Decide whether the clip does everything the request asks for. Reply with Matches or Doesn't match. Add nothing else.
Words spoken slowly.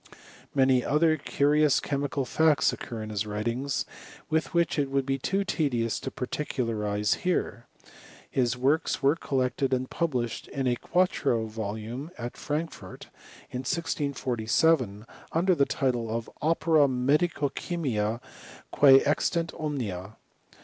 Matches